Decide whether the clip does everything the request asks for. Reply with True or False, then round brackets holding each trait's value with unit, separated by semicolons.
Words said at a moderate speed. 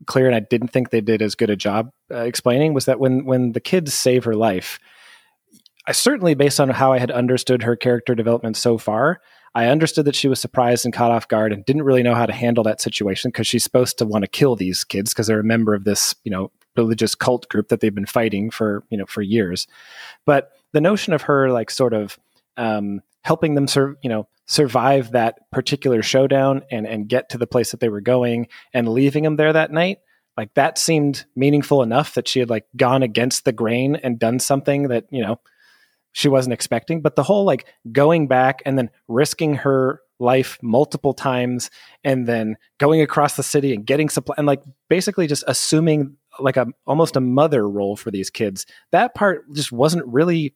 False (215 wpm)